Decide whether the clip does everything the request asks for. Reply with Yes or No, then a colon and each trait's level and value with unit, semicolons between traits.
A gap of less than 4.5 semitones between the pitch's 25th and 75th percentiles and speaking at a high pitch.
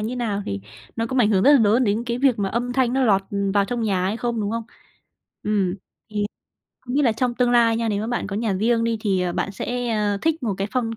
Yes: average, 3.2 semitones; high, 230 Hz